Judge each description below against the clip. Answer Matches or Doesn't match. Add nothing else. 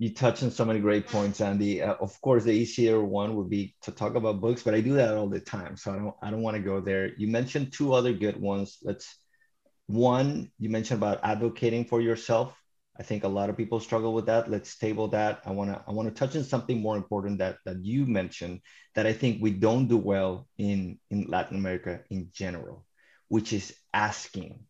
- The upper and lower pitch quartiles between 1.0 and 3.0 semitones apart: Matches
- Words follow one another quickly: Matches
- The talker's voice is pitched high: Doesn't match